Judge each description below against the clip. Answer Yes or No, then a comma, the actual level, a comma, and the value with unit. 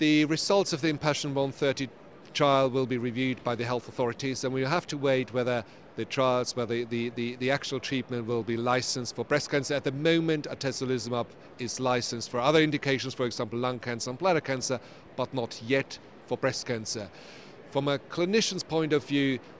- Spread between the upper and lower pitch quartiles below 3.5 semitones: Yes, average, 3.0 semitones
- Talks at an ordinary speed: Yes, average, 195 wpm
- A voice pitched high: No, low, 130 Hz